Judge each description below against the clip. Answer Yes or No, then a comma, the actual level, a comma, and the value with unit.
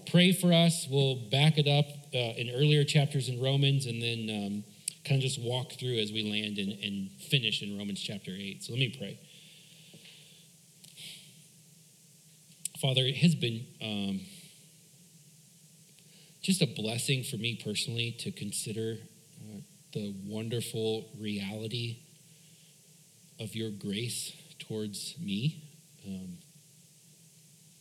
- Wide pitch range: Yes, wide, 5.8 semitones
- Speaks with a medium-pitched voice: Yes, medium, 150 Hz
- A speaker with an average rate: No, slow, 125 wpm